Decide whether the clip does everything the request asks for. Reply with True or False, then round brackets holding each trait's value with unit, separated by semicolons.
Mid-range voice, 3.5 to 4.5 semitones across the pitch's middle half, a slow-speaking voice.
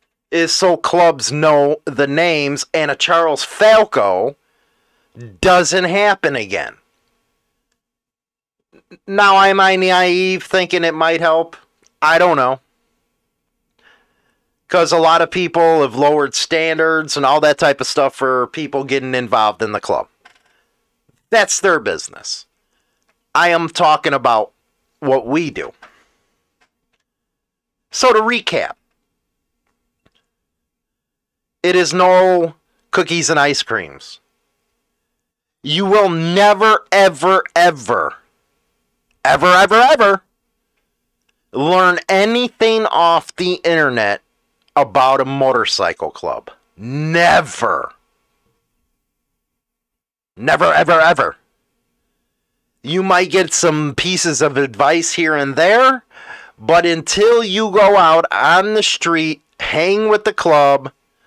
True (170 Hz; 4.1 semitones; 105 wpm)